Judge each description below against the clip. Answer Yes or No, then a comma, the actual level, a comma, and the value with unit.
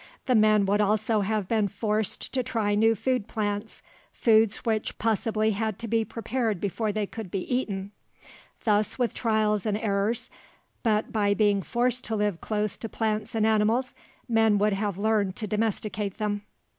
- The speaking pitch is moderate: No, high, 215 Hz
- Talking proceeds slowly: No, average, 170 wpm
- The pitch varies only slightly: Yes, narrow, 1.5 semitones